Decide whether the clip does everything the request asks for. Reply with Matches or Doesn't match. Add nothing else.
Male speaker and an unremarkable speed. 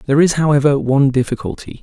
Matches